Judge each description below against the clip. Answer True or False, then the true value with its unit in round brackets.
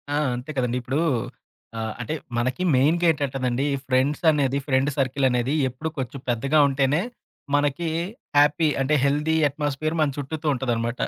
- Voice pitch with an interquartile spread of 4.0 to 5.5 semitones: False (2.6 semitones)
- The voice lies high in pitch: False (140 Hz)